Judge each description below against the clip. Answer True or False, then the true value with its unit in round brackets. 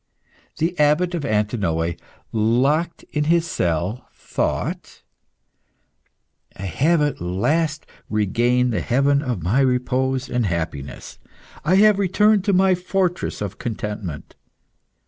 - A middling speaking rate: False (115 wpm)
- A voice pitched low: True (130 Hz)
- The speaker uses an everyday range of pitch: False (8.1 semitones)